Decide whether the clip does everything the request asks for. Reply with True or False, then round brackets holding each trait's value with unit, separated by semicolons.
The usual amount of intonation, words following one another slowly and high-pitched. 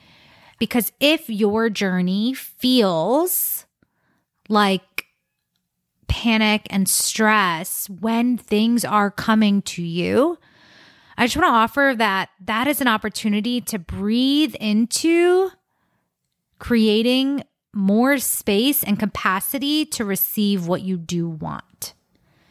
True (3.9 semitones; 105 wpm; 220 Hz)